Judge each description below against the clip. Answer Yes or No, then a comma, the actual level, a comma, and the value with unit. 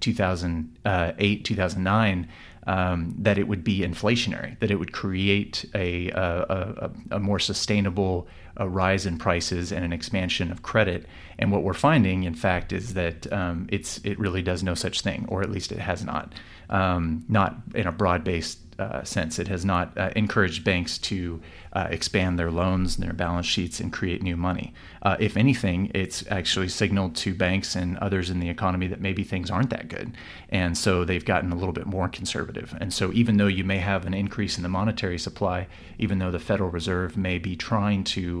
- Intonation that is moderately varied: No, narrow, 2.3 semitones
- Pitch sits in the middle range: No, very low, 95 Hz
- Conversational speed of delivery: Yes, average, 195 wpm